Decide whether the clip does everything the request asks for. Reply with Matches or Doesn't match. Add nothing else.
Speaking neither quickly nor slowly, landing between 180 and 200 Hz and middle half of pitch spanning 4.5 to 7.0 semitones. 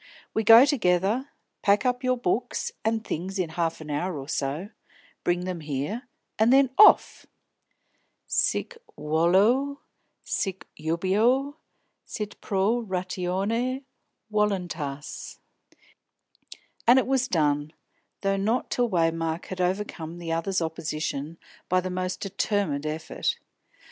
Doesn't match